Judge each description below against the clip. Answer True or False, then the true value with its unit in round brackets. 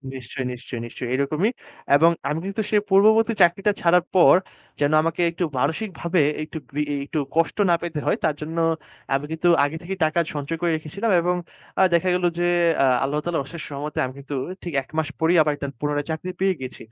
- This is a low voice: False (160 Hz)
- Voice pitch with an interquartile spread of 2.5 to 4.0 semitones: True (3.5 semitones)